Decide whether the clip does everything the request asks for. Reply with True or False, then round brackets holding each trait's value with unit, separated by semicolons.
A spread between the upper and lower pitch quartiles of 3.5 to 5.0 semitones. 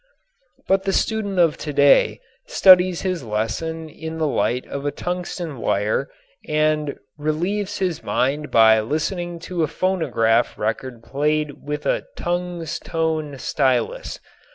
True (4.4 semitones)